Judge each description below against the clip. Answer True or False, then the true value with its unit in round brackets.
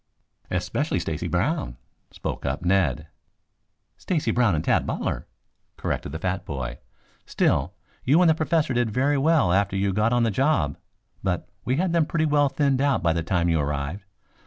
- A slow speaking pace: False (175 wpm)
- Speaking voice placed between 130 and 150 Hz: False (105 Hz)